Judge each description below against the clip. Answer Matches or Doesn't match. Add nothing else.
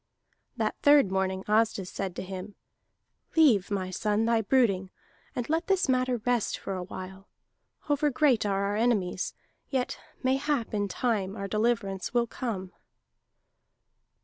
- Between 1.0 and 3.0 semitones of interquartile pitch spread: Doesn't match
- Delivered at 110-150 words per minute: Matches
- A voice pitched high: Matches